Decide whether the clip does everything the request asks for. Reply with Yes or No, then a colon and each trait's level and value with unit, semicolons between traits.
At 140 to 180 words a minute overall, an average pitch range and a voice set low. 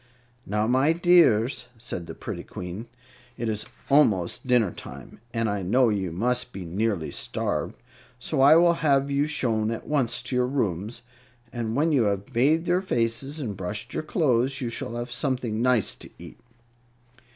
Yes: average, 170 wpm; average, 4.3 semitones; low, 120 Hz